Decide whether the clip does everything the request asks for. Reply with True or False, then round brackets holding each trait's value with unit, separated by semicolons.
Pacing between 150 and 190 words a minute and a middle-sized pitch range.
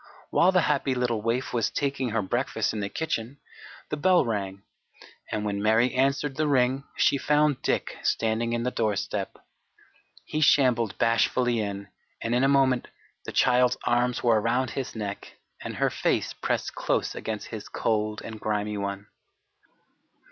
True (160 wpm; 3.9 semitones)